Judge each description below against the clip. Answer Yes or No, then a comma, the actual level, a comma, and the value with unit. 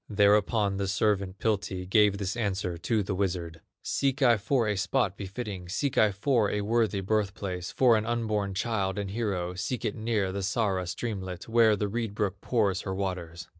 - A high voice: No, low, 100 Hz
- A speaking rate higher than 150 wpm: Yes, average, 185 wpm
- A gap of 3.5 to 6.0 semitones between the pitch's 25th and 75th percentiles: No, narrow, 2.6 semitones